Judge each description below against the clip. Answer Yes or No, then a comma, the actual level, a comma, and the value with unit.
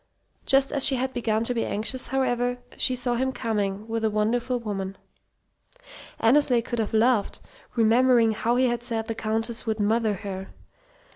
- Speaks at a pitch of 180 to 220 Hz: No, high, 230 Hz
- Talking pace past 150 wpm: Yes, average, 165 wpm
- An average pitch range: No, narrow, 2.3 semitones